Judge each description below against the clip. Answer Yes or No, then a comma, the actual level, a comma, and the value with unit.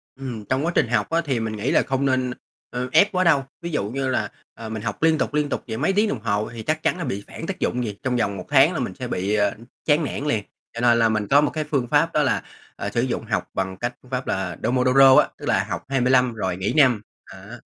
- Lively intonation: No, average, 4.9 semitones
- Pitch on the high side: No, low, 125 Hz